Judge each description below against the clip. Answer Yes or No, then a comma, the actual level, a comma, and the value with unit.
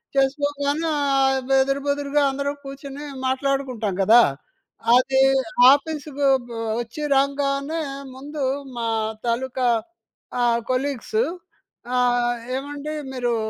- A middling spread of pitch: No, narrow, 2.1 semitones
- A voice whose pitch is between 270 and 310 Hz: Yes, very high, 275 Hz